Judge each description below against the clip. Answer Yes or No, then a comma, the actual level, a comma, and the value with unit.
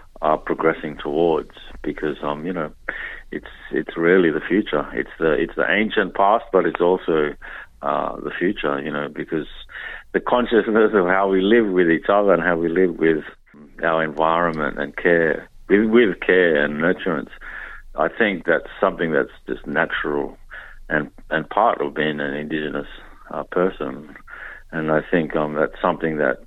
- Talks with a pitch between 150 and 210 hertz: No, very low, 80 Hz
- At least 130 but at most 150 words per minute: No, average, 165 wpm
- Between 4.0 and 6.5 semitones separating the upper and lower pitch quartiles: No, narrow, 2.4 semitones